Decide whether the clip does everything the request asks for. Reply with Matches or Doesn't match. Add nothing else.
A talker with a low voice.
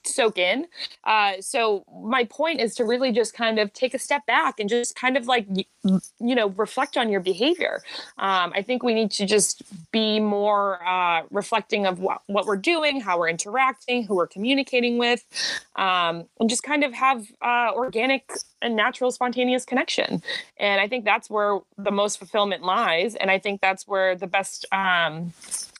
Doesn't match